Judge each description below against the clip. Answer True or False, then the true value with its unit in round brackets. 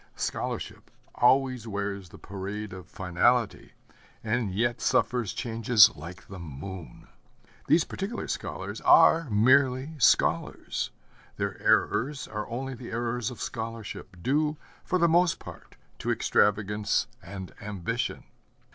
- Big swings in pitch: False (4.3 semitones)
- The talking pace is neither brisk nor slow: False (120 wpm)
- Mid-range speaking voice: False (115 Hz)